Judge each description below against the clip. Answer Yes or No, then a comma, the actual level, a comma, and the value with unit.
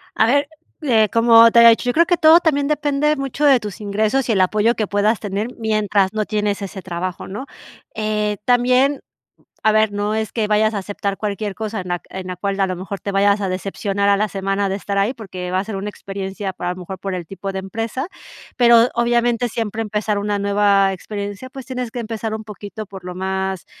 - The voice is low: No, high, 210 Hz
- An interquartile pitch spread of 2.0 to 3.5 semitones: Yes, average, 2.8 semitones